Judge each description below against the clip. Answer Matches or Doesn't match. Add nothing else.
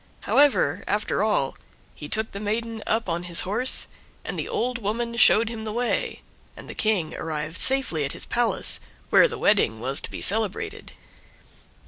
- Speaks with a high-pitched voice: Matches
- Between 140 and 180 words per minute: Matches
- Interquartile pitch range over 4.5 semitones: Matches